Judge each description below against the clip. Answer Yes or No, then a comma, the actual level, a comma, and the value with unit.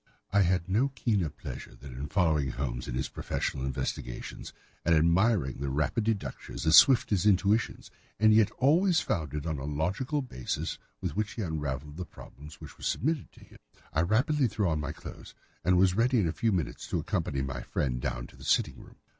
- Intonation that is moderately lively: No, wide, 7.2 semitones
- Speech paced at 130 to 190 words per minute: No, average, 200 wpm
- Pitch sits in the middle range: No, very low, 85 Hz